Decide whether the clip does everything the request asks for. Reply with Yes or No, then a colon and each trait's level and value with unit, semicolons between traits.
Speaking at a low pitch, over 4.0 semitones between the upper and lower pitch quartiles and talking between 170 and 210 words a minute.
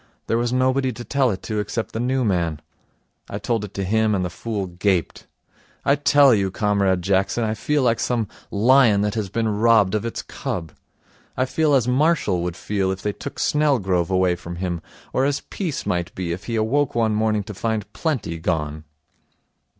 Yes: low, 105 Hz; average, 4.7 semitones; average, 190 wpm